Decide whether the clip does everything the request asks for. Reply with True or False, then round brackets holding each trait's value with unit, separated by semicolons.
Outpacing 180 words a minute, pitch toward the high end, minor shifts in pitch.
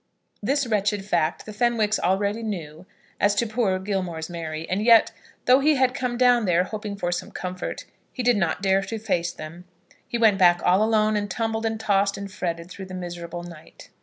False (195 wpm; 200 Hz; 3.9 semitones)